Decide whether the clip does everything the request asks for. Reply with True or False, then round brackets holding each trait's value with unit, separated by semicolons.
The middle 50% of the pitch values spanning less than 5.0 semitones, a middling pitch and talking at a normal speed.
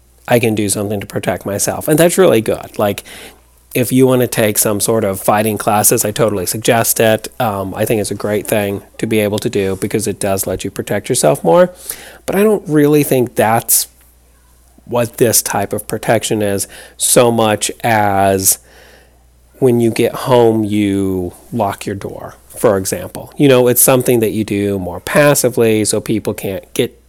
False (3.7 semitones; 110 Hz; 185 wpm)